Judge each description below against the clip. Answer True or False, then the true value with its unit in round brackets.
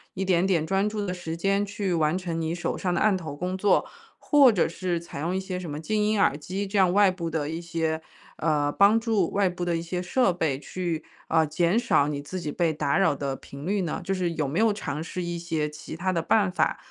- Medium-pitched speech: True (175 Hz)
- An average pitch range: True (3.3 semitones)